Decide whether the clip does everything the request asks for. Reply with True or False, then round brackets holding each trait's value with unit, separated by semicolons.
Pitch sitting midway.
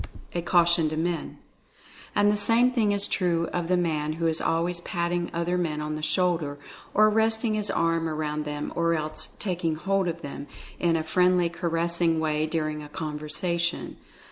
True (170 Hz)